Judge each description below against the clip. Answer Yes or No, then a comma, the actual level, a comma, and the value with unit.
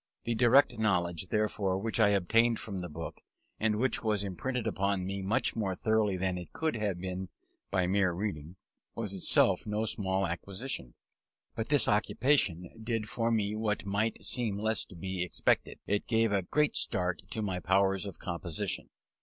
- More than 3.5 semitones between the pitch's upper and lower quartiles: No, average, 3.1 semitones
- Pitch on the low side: Yes, low, 100 Hz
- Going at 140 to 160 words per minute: No, average, 170 wpm